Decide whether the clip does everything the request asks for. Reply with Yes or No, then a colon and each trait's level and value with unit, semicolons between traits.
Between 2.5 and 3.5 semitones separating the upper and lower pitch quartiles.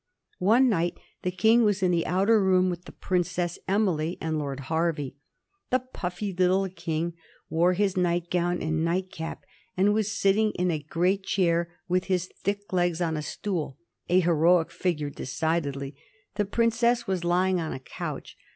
Yes: average, 2.8 semitones